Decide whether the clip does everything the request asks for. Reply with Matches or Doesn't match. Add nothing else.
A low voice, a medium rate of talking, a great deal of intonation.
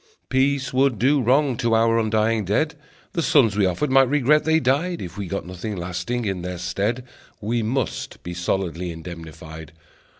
Matches